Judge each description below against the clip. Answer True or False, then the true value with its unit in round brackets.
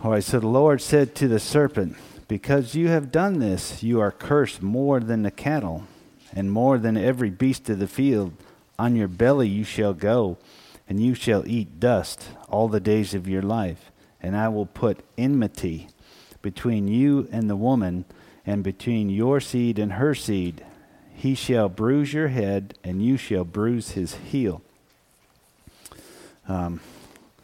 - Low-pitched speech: True (110 Hz)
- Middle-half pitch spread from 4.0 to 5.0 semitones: True (4.6 semitones)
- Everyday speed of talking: True (165 wpm)